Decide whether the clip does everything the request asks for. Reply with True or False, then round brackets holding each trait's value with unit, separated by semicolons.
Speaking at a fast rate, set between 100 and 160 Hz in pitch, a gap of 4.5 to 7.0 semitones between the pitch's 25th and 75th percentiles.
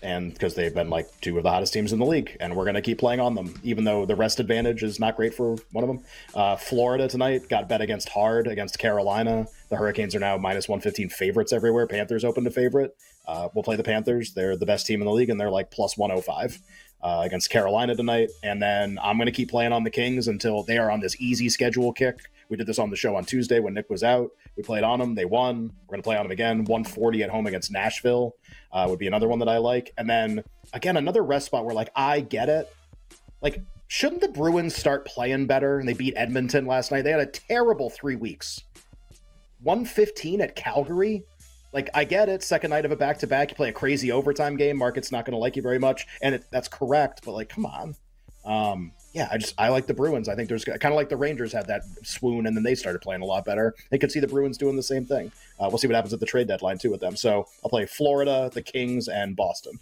False (250 wpm; 120 Hz; 3.8 semitones)